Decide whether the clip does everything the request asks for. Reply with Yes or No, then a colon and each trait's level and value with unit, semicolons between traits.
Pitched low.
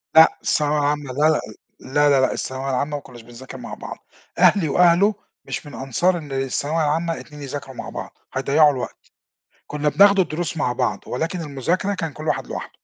No: medium, 150 Hz